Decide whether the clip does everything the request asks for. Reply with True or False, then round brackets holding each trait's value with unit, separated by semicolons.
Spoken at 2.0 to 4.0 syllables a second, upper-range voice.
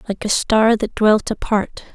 False (4.2 syllables/s; 215 Hz)